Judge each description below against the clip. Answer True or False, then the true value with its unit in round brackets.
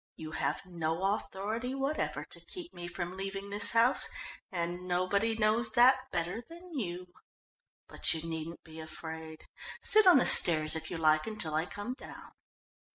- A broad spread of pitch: True (5.8 semitones)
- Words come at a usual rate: True (160 wpm)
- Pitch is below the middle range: False (185 Hz)